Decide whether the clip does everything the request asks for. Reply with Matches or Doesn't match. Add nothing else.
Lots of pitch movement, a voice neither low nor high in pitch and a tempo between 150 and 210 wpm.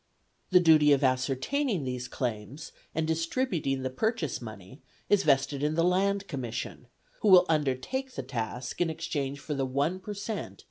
Matches